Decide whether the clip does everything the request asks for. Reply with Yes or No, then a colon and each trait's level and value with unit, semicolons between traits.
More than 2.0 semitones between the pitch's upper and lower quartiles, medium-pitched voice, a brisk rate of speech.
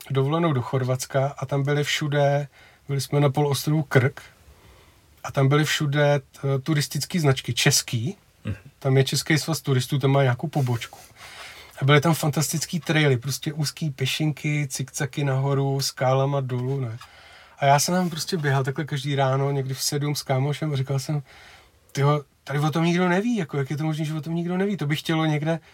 Yes: narrow, 2.4 semitones; medium, 145 Hz; fast, 185 wpm